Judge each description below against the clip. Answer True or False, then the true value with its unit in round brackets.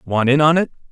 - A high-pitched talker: False (140 Hz)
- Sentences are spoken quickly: True (260 wpm)